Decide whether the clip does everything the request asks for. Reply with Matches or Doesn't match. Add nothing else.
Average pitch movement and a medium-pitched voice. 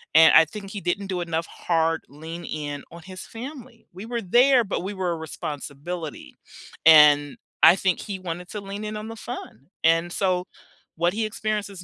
Matches